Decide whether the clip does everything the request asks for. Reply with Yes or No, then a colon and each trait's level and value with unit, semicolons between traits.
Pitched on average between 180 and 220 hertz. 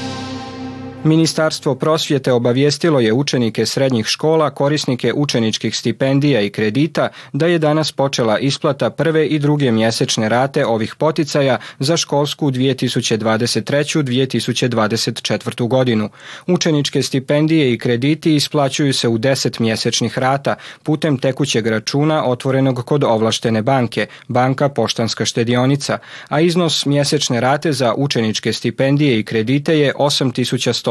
No: low, 135 Hz